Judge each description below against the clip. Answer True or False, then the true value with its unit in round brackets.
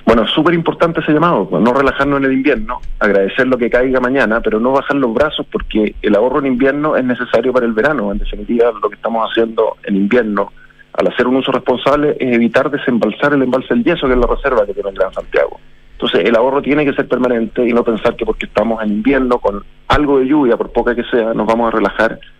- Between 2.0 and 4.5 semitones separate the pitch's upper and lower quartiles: True (3.2 semitones)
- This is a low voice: True (125 Hz)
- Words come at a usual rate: False (230 wpm)